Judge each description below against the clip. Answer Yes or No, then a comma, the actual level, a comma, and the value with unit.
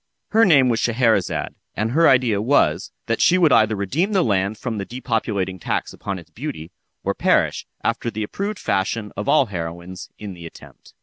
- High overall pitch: No, low, 110 Hz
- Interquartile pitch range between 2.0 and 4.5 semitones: No, average, 5.0 semitones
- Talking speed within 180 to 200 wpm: Yes, average, 185 wpm